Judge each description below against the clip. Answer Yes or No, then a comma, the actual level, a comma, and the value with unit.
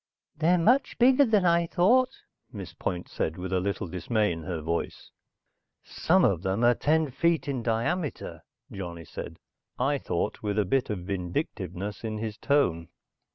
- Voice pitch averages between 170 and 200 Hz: No, low, 110 Hz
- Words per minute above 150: Yes, average, 160 wpm